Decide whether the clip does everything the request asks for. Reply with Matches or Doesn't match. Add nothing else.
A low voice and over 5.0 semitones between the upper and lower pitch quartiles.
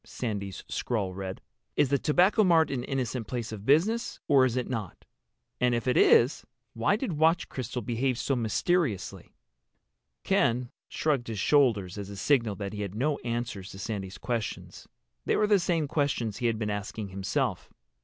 Matches